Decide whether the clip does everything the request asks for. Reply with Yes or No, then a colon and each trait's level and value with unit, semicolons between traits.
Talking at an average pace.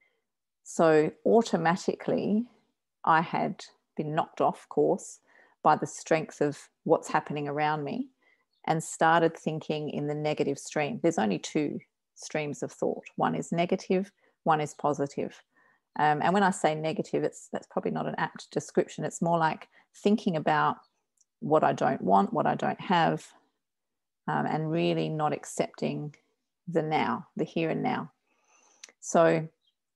Yes: average, 145 wpm